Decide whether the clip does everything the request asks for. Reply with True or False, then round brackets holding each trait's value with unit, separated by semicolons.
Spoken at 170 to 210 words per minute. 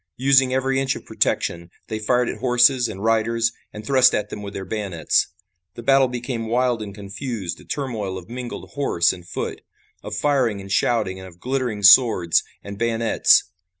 True (180 wpm)